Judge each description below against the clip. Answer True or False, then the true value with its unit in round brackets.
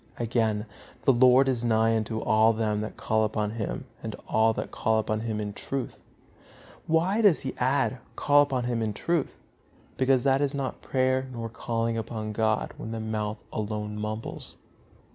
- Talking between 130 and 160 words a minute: False (170 wpm)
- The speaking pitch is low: True (115 Hz)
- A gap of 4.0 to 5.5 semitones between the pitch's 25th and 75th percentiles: False (3.2 semitones)